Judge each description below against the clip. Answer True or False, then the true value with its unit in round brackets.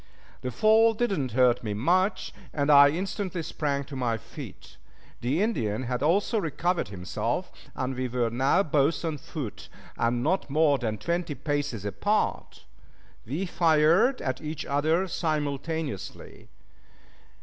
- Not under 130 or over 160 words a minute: True (140 wpm)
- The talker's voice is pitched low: False (145 Hz)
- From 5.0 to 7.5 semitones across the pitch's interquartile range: True (5.3 semitones)